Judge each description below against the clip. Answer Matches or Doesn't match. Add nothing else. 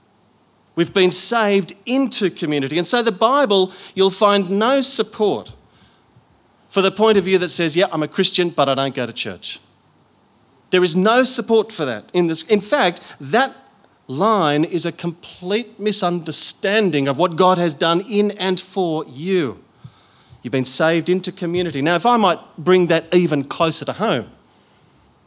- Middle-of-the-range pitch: Matches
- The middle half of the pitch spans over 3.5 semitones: Matches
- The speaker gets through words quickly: Doesn't match